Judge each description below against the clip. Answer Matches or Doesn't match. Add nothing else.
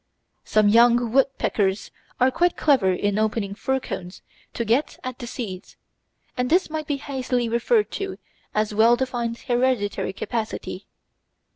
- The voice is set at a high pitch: Matches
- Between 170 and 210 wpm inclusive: Doesn't match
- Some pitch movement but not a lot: Matches